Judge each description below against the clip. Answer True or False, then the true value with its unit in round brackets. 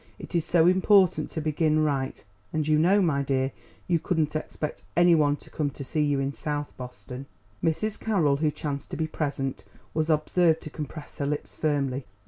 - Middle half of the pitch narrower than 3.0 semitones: True (2.5 semitones)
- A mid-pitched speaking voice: True (155 Hz)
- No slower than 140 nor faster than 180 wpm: False (190 wpm)